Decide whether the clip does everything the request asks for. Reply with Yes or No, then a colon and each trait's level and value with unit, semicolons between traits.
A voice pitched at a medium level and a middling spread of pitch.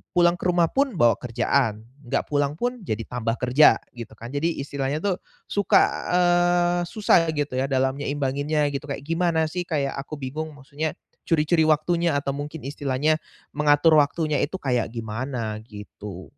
Yes: medium, 145 Hz; average, 4.1 semitones